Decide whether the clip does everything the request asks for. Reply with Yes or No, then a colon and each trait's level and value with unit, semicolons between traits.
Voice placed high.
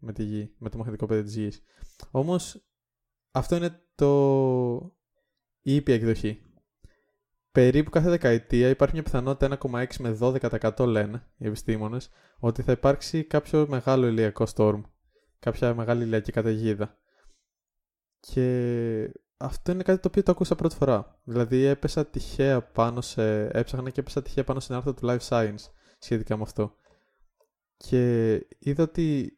No: low, 125 Hz